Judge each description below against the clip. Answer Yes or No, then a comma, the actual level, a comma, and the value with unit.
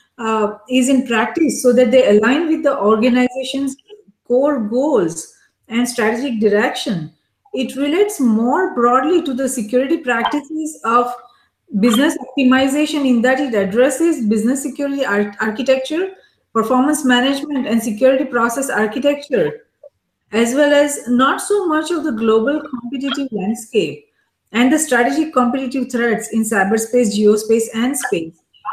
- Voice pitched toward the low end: No, very high, 255 Hz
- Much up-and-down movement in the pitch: No, average, 3.7 semitones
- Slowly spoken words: Yes, slow, 130 wpm